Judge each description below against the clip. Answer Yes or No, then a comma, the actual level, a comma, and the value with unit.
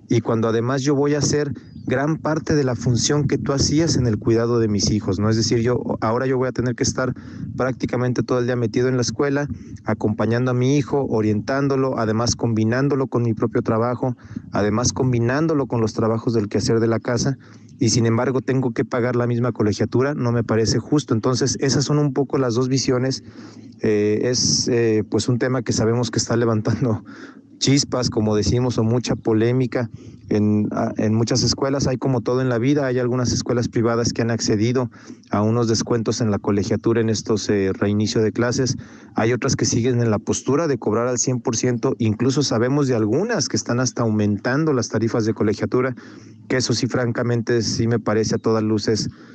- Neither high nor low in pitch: No, low, 120 Hz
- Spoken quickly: Yes, fast, 195 wpm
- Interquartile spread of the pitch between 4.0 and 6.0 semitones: No, narrow, 2.4 semitones